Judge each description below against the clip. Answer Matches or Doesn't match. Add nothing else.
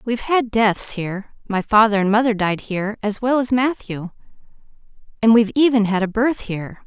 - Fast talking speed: Doesn't match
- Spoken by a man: Doesn't match